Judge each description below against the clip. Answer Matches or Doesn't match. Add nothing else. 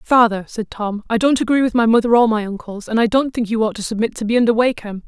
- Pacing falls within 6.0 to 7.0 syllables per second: Matches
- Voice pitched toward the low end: Doesn't match